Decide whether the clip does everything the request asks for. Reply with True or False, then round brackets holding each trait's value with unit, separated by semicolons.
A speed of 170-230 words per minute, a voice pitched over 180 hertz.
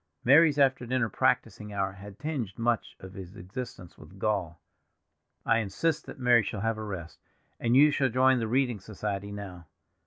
False (175 wpm; 110 Hz)